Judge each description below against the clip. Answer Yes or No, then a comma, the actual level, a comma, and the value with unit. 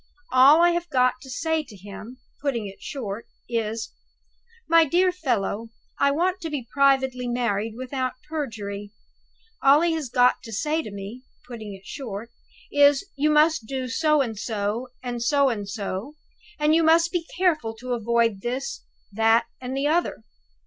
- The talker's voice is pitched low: No, very high, 255 Hz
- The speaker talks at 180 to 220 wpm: No, average, 165 wpm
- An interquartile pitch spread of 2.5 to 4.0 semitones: No, average, 5.2 semitones